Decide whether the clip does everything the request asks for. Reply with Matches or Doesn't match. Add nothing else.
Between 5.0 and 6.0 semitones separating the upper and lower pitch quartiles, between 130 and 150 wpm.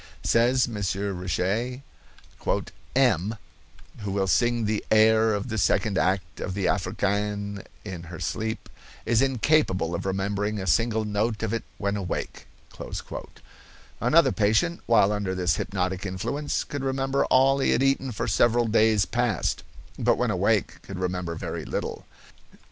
Doesn't match